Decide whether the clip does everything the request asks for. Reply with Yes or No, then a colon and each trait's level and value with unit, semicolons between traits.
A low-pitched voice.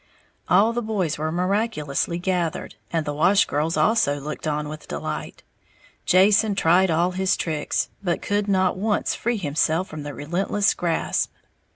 No: medium, 175 Hz